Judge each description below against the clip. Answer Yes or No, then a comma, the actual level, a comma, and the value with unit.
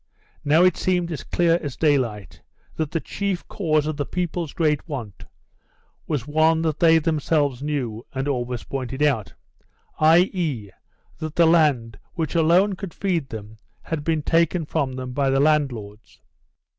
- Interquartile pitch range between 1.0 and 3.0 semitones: No, average, 3.8 semitones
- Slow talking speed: No, average, 155 wpm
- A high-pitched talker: No, medium, 150 Hz